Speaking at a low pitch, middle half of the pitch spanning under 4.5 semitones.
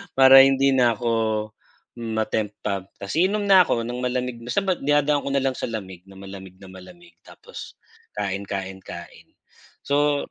No: low, 120 Hz; wide, 6.2 semitones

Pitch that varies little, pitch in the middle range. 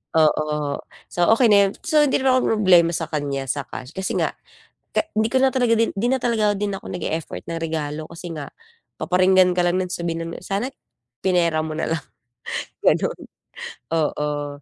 No: average, 5.0 semitones; medium, 175 Hz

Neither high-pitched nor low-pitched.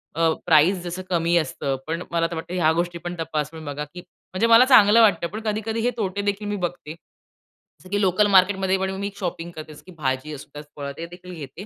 Yes: medium, 175 Hz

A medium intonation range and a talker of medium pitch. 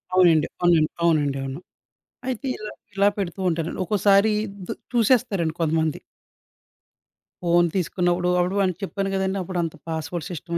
Yes: average, 3.2 semitones; medium, 175 Hz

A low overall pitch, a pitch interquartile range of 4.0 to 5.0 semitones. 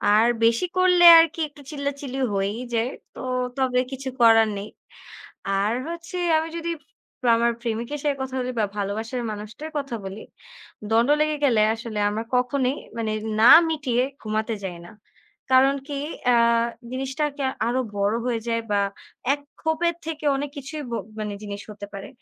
No: very high, 250 Hz; average, 4.6 semitones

